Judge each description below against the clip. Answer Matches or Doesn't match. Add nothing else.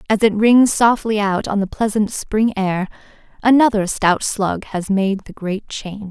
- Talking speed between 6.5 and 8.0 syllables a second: Doesn't match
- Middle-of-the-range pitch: Doesn't match